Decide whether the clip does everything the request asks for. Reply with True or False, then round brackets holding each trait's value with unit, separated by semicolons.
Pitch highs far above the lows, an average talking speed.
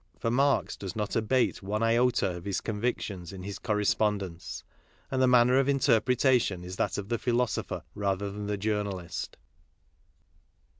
False (3.7 semitones; 160 wpm)